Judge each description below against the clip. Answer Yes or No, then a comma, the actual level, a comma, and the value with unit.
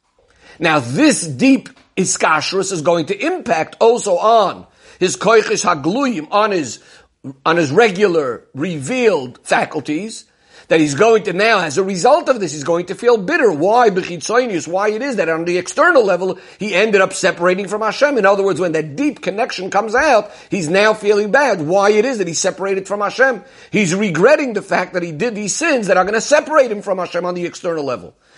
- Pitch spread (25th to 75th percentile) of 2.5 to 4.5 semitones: No, average, 4.9 semitones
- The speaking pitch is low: No, high, 200 Hz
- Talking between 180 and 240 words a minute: Yes, average, 195 wpm